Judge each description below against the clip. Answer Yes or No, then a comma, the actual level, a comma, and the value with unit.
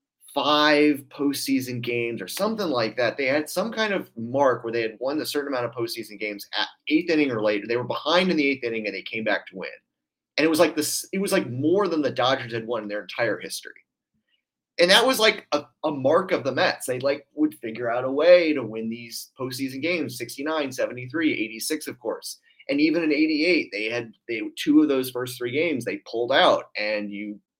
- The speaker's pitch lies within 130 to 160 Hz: Yes, medium, 140 Hz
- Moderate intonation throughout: No, wide, 6.6 semitones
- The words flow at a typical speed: No, fast, 225 wpm